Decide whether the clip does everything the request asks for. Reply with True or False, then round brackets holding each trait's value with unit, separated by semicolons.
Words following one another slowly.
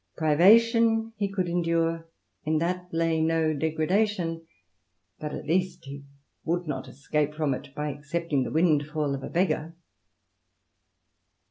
True (130 wpm)